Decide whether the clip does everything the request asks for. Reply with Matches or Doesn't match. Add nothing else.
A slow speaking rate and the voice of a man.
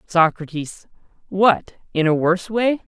Matches